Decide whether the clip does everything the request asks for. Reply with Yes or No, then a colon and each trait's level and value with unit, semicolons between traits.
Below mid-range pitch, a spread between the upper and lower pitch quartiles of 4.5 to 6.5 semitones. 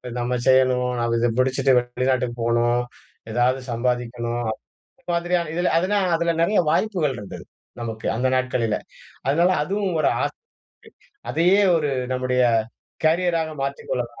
Yes: low, 130 Hz; wide, 5.6 semitones